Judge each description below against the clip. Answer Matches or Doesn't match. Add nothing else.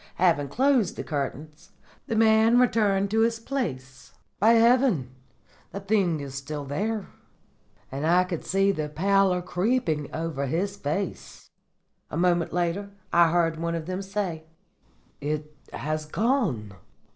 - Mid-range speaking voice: Matches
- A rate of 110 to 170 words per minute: Matches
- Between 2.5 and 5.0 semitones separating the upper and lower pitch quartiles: Doesn't match